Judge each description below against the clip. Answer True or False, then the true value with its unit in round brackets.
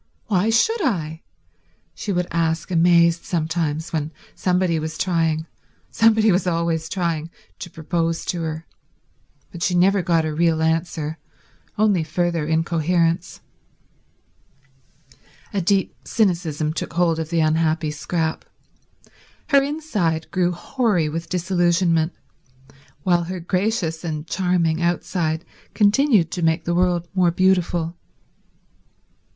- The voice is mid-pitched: True (170 Hz)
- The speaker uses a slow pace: True (115 wpm)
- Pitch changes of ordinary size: False (2.2 semitones)